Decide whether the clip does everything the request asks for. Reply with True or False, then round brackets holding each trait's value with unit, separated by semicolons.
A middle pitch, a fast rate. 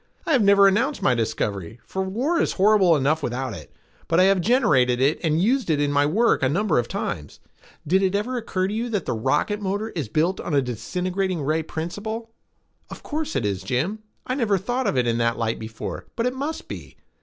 True (180 Hz; 220 wpm)